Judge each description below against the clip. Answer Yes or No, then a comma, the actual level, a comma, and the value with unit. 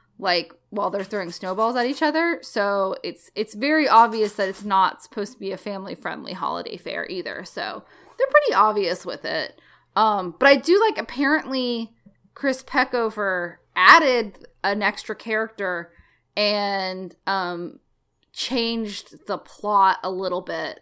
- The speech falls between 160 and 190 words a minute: No, average, 145 wpm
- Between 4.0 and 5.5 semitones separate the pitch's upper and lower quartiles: Yes, average, 4.4 semitones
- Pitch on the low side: No, high, 210 Hz